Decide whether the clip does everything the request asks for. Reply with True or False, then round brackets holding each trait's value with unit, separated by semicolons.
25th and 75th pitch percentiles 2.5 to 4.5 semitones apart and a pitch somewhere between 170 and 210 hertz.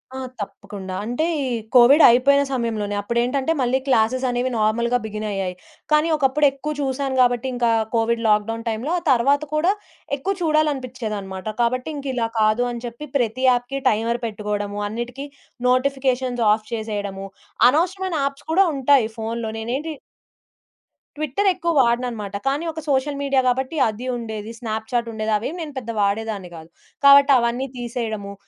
False (3.9 semitones; 245 Hz)